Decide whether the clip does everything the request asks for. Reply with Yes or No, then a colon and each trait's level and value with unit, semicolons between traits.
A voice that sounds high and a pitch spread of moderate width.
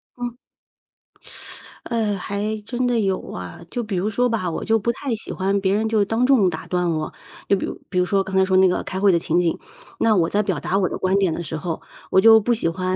Yes: high, 195 Hz; average, 3.5 semitones